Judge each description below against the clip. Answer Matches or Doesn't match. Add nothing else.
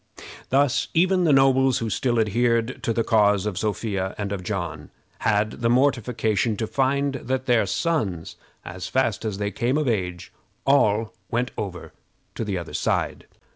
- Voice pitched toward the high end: Doesn't match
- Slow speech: Doesn't match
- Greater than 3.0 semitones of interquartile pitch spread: Matches